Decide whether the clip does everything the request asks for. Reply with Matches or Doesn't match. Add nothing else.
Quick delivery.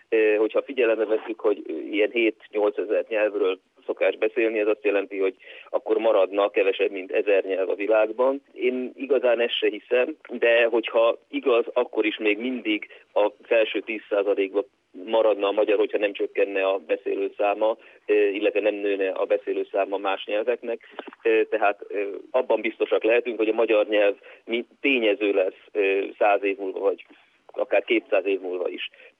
Doesn't match